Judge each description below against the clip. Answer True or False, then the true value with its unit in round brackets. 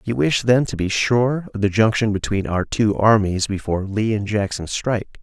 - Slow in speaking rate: False (205 wpm)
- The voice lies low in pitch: True (105 Hz)